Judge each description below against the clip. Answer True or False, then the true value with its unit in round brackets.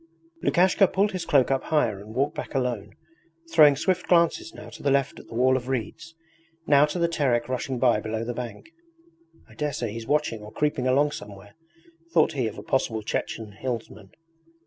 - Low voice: True (130 Hz)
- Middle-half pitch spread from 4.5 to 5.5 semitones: True (4.8 semitones)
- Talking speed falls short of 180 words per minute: False (190 wpm)